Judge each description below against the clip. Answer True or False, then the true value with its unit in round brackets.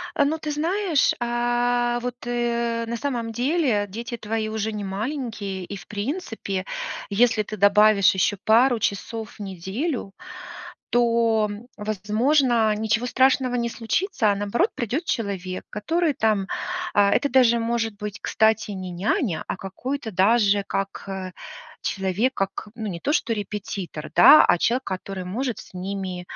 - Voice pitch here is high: True (220 Hz)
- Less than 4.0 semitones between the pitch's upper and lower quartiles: True (3.4 semitones)